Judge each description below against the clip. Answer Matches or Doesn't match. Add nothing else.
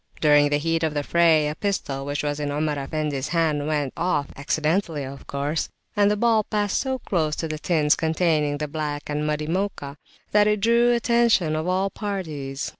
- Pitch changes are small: Doesn't match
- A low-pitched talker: Doesn't match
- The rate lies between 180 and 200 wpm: Matches